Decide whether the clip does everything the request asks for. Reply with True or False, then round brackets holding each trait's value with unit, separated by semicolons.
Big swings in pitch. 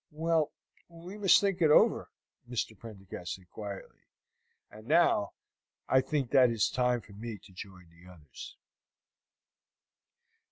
True (7.7 semitones)